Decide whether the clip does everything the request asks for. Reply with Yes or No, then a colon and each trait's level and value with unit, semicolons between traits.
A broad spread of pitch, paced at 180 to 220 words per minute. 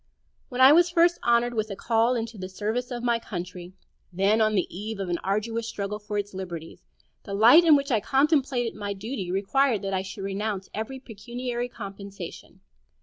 No: average, 3.8 semitones; average, 190 wpm